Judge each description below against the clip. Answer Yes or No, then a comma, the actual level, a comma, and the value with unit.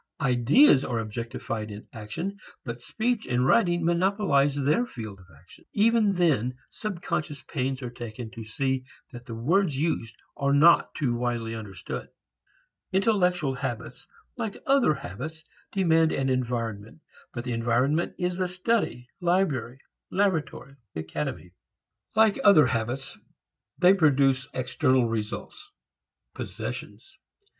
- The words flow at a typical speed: No, slow, 125 wpm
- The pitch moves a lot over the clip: Yes, wide, 7.1 semitones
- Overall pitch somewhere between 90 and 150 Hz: Yes, low, 135 Hz